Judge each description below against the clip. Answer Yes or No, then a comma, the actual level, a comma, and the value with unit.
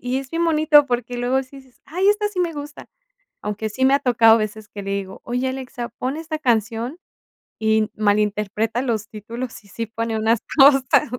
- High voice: Yes, high, 245 Hz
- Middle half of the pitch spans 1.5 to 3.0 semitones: No, average, 4.1 semitones